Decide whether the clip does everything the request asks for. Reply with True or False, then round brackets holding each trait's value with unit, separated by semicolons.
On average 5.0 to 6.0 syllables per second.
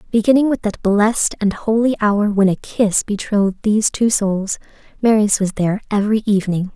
True (5.6 syllables/s)